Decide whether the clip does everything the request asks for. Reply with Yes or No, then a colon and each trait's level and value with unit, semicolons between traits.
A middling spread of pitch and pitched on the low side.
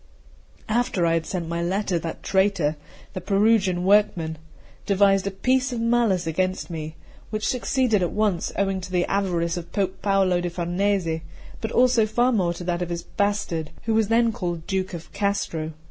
No: average, 3.5 semitones; high, 190 Hz